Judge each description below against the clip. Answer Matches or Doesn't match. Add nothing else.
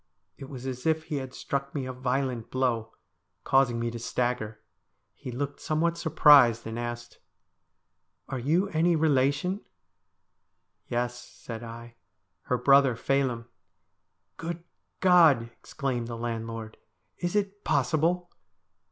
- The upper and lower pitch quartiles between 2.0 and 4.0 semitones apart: Doesn't match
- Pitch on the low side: Matches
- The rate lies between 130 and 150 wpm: Matches